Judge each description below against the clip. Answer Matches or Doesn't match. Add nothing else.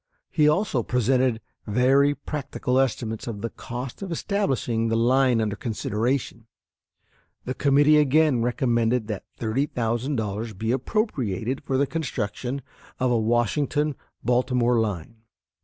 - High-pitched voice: Doesn't match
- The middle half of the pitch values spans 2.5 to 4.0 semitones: Matches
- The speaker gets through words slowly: Matches